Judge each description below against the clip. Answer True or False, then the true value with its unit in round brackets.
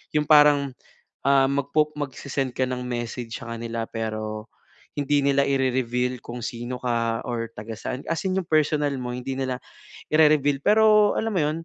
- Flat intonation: False (3.6 semitones)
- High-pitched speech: False (135 Hz)